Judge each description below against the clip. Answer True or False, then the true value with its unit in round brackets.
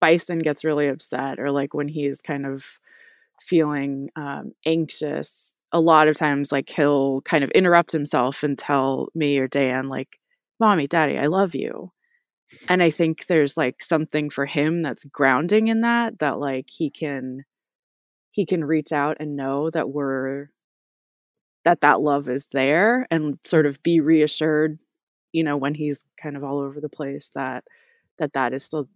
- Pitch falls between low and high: True (150 Hz)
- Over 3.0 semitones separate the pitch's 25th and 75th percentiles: False (2.7 semitones)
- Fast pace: False (170 wpm)